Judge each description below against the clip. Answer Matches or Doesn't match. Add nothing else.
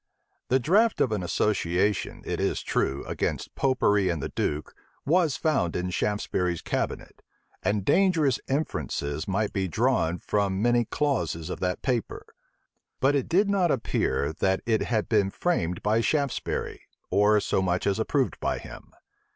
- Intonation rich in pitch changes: Matches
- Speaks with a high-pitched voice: Doesn't match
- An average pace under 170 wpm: Matches